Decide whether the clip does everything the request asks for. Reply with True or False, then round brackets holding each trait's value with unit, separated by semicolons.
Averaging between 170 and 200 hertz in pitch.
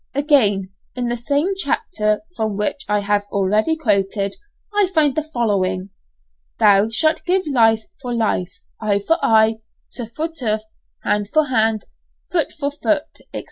False (225 Hz)